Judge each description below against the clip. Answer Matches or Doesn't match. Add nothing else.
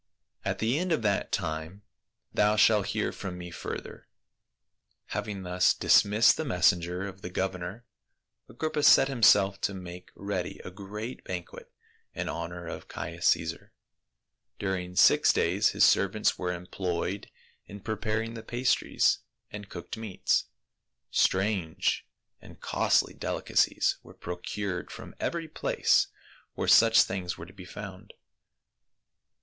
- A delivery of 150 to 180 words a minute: Doesn't match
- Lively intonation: Doesn't match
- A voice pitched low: Matches